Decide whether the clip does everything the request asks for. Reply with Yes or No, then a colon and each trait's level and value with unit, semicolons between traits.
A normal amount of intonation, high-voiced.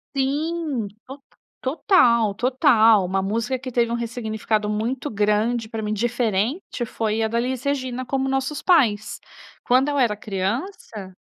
Yes: average, 3.7 semitones; high, 235 Hz